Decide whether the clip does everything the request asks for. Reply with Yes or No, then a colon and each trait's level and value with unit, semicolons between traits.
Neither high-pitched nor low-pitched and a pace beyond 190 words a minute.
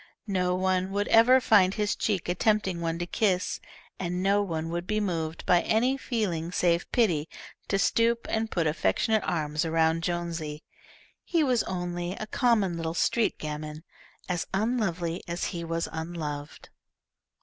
No: medium, 180 Hz; average, 155 wpm